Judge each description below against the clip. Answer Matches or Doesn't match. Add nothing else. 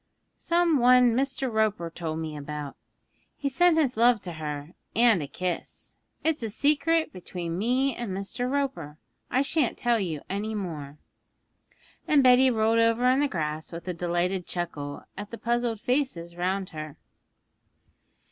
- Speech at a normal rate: Matches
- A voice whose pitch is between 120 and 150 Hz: Doesn't match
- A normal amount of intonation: Doesn't match